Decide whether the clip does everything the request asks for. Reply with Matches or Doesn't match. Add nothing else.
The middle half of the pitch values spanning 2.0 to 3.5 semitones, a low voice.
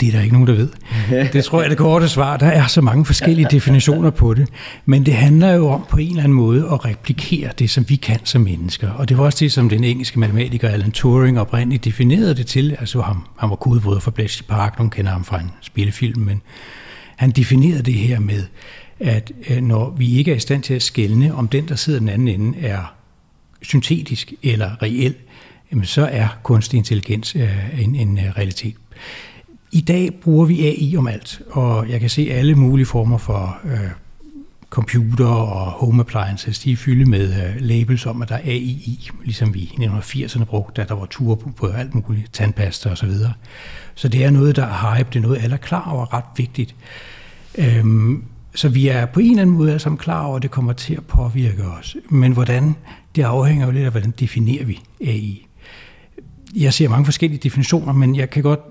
Doesn't match